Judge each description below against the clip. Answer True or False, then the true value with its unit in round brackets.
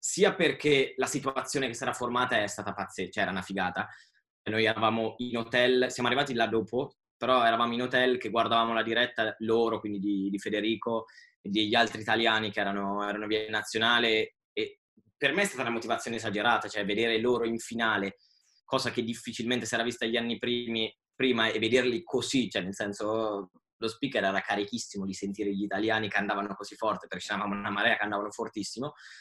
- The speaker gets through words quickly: True (190 wpm)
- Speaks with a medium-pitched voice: False (115 Hz)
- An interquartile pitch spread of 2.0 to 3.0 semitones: True (2.5 semitones)